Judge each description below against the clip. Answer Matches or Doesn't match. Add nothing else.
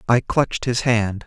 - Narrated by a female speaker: Doesn't match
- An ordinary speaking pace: Matches